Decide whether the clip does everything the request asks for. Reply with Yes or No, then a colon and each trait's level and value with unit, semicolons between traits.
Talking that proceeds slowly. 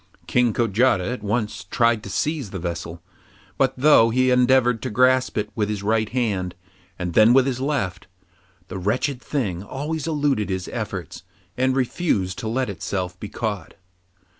No: average, 165 wpm